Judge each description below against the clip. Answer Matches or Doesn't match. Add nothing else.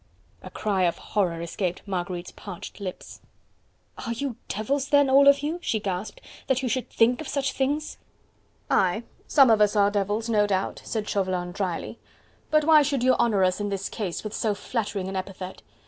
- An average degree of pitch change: Doesn't match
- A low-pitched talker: Doesn't match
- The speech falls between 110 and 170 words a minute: Doesn't match